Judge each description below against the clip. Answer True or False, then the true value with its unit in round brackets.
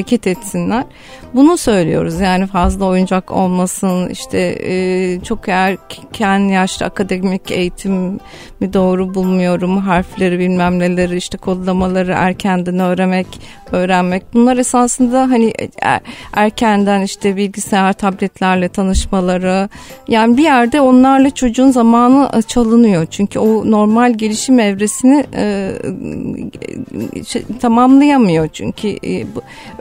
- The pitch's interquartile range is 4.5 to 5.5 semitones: False (3.9 semitones)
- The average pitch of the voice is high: True (195 Hz)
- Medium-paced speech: True (105 wpm)